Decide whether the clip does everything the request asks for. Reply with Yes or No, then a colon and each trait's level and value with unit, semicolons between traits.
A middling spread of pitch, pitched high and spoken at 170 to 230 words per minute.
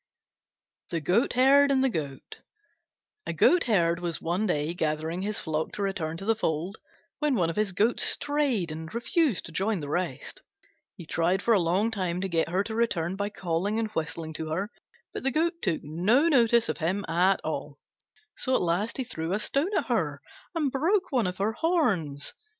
No: wide, 6.0 semitones; high, 195 Hz; average, 190 wpm